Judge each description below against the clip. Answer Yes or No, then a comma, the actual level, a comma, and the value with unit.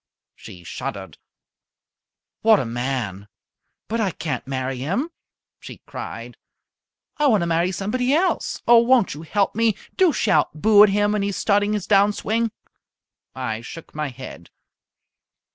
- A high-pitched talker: Yes, high, 195 Hz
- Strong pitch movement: Yes, wide, 8.7 semitones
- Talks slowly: No, average, 150 wpm